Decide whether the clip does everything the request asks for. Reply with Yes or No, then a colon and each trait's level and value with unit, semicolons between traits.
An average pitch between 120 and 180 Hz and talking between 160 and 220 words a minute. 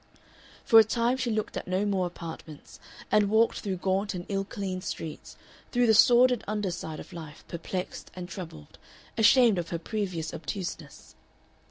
No: high, 195 Hz; average, 165 wpm